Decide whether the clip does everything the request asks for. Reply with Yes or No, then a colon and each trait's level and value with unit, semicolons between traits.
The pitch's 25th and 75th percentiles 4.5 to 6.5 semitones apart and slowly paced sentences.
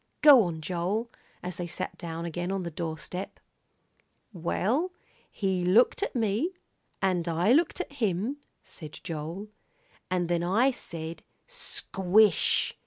Yes: average, 4.8 semitones; slow, 130 wpm